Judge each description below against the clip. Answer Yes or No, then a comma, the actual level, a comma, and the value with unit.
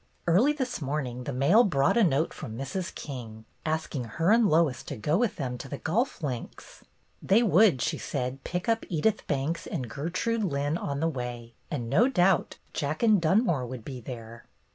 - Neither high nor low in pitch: Yes, medium, 150 Hz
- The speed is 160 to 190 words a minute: Yes, average, 185 wpm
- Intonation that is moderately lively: No, wide, 6.8 semitones